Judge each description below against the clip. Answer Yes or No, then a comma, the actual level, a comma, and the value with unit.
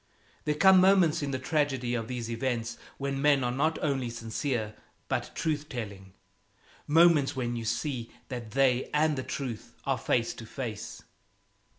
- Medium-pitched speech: No, low, 130 Hz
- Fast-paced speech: No, average, 160 wpm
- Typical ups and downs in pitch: Yes, average, 4.0 semitones